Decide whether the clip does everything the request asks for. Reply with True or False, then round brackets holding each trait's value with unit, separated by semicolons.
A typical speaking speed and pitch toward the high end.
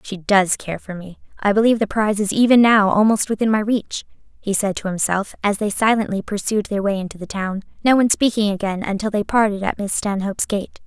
False (220 wpm; 205 Hz)